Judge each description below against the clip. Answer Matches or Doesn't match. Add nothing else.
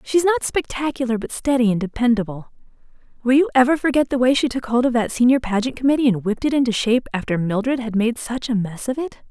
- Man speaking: Doesn't match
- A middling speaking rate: Doesn't match